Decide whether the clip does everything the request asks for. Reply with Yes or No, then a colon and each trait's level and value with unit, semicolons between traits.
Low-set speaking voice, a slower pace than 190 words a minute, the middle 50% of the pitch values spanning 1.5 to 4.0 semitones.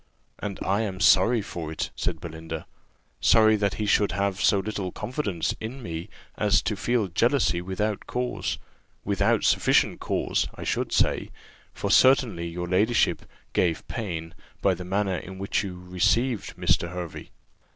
Yes: very low, 95 Hz; average, 150 wpm; average, 3.5 semitones